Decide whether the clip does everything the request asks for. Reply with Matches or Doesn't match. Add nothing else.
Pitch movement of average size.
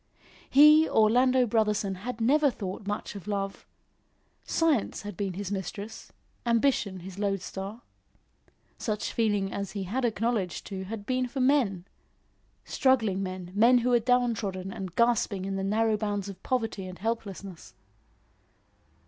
Matches